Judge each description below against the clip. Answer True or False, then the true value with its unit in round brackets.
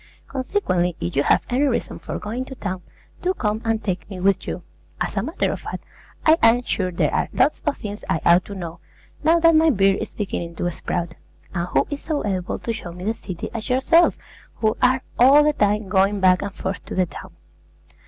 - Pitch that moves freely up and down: True (6.0 semitones)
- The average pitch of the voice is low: False (205 Hz)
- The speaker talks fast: True (220 wpm)